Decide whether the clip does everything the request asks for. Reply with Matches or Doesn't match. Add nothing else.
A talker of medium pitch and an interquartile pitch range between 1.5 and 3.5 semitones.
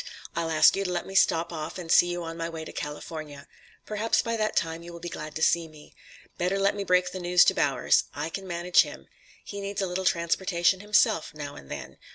Matches